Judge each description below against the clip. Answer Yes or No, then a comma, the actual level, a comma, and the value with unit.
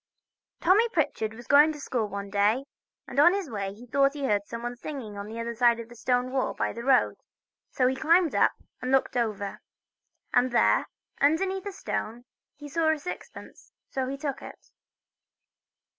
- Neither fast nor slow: Yes, average, 185 wpm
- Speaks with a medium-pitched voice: No, very high, 255 Hz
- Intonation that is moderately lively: Yes, average, 4.2 semitones